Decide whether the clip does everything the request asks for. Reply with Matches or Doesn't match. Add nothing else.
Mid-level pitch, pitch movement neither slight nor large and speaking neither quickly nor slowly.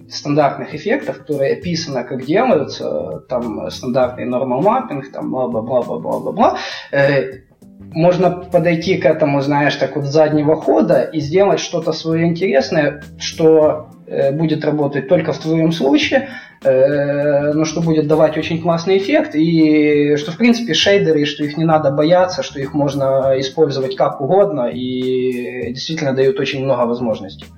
Matches